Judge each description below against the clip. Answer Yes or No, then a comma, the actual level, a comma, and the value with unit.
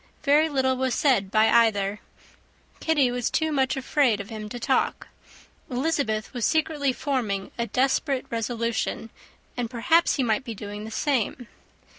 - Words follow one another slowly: No, average, 150 wpm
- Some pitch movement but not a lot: Yes, average, 4.0 semitones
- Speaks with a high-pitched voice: Yes, high, 245 Hz